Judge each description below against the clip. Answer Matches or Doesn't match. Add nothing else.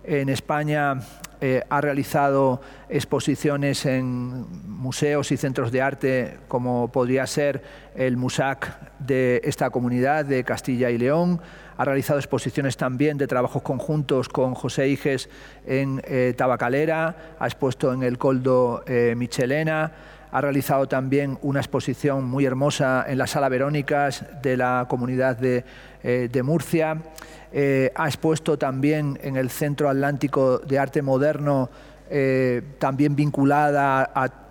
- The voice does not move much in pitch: Matches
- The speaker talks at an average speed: Matches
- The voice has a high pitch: Doesn't match